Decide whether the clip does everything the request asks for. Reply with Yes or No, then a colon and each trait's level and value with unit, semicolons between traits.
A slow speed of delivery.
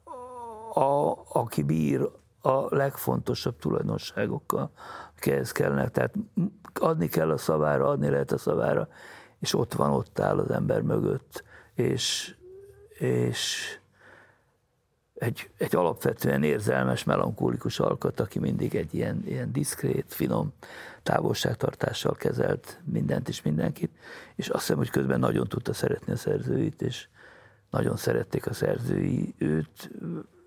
No: average, 120 wpm